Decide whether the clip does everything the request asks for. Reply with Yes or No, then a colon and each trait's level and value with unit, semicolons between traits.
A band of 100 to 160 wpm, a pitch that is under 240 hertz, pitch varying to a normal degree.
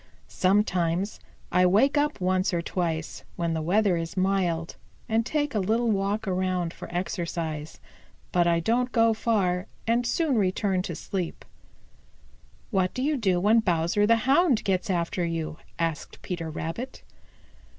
Yes: average, 150 wpm; medium, 185 Hz; average, 4.6 semitones